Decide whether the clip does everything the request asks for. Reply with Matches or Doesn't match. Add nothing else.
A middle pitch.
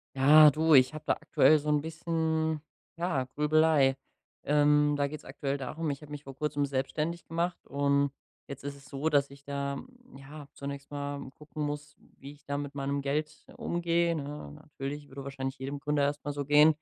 Matches